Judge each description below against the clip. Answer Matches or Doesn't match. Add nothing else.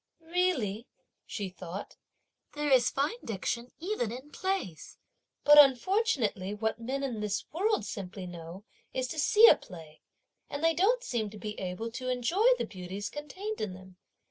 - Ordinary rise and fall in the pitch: Doesn't match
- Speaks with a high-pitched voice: Matches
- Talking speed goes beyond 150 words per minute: Matches